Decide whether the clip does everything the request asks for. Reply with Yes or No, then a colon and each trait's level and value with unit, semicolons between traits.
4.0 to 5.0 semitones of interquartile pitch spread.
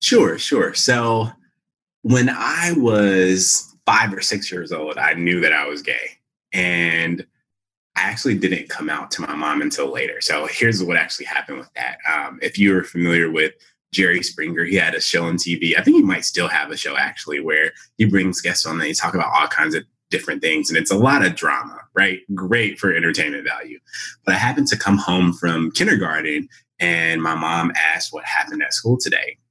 Yes: average, 4.5 semitones